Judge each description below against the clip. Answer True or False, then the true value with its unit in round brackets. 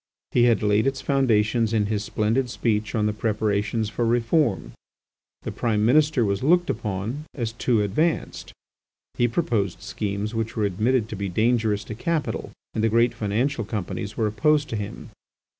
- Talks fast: False (165 wpm)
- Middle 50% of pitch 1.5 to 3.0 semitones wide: True (2.6 semitones)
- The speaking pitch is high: False (110 Hz)